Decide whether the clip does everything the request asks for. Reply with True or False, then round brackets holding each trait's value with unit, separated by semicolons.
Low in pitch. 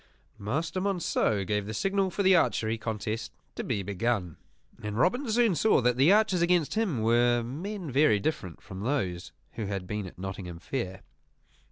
True (120 Hz)